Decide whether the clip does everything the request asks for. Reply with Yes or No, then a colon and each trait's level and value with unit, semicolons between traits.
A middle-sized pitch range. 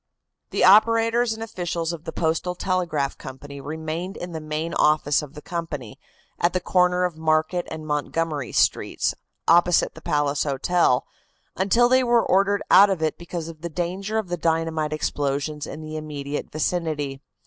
Yes: average, 3.0 semitones